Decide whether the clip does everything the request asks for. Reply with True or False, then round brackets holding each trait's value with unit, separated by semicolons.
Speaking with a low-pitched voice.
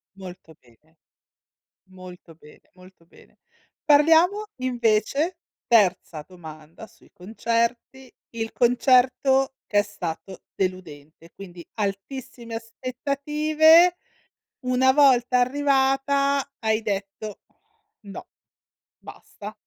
False (230 Hz)